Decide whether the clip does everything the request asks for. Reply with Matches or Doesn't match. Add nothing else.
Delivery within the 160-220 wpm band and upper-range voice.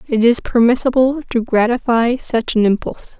Doesn't match